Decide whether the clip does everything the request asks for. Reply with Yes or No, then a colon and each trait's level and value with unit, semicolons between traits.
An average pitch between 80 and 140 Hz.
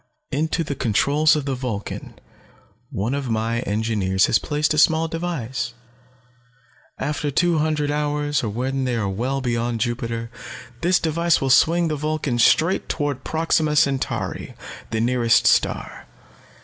Yes: low, 135 Hz